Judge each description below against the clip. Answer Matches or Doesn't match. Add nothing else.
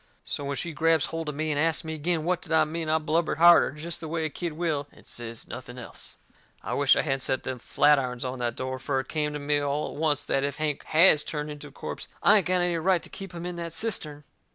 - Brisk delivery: Matches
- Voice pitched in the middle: Matches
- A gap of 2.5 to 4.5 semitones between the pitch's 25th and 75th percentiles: Matches